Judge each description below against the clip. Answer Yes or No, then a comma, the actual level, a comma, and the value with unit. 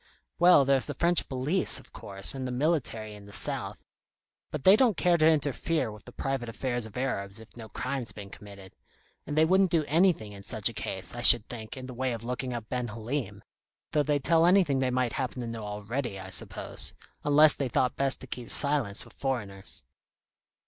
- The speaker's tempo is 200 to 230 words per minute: Yes, fast, 205 wpm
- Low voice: Yes, low, 125 Hz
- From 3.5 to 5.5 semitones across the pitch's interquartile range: Yes, average, 5.0 semitones